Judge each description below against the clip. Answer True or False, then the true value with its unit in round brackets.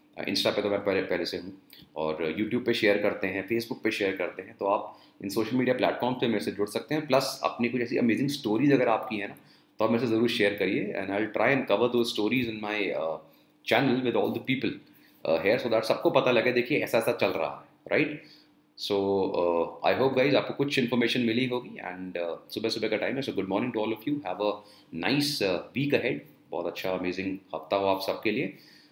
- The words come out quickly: True (235 wpm)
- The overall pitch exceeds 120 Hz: False (110 Hz)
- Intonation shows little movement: False (3.7 semitones)